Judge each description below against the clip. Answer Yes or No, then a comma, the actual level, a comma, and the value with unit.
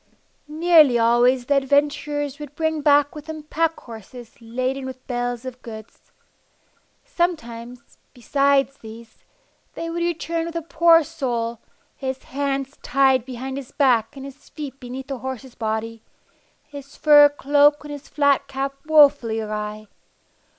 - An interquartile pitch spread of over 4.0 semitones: No, average, 3.3 semitones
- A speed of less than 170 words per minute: Yes, average, 140 wpm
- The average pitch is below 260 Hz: No, very high, 275 Hz